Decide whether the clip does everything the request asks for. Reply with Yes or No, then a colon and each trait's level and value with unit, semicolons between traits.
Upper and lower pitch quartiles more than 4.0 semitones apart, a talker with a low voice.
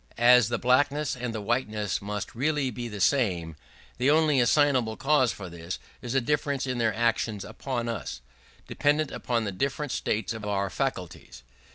Yes: average, 4.6 semitones; low, 120 Hz